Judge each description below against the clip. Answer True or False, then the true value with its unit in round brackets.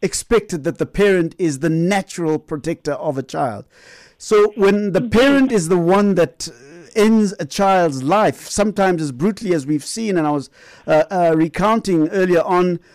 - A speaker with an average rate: True (170 wpm)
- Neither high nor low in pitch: True (180 Hz)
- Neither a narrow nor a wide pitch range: True (4.1 semitones)